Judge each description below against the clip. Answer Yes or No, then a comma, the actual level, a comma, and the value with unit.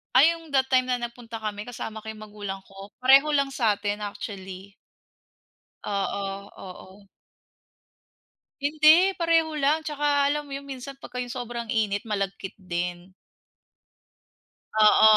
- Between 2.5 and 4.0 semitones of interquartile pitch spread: No, wide, 5.6 semitones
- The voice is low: No, high, 230 Hz